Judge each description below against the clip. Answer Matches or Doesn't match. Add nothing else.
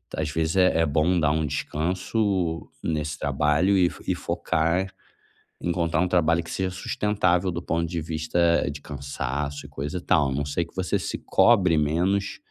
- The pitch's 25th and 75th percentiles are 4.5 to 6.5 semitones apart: Doesn't match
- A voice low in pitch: Matches